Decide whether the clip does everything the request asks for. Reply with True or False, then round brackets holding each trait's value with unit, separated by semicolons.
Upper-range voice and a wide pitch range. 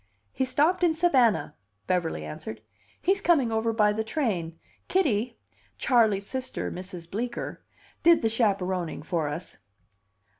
True (220 Hz; 6.3 semitones)